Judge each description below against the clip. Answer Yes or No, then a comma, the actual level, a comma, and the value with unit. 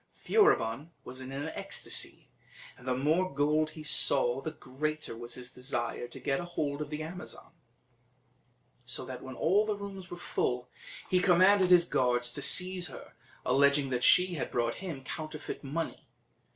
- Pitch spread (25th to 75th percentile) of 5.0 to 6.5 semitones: Yes, wide, 5.4 semitones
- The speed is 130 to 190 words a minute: Yes, average, 160 wpm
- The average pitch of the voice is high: No, medium, 150 Hz